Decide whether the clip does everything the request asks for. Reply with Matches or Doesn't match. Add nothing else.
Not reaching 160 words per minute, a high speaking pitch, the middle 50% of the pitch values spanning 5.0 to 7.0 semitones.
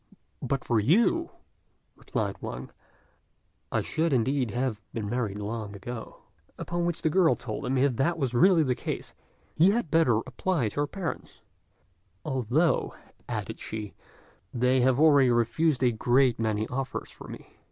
Doesn't match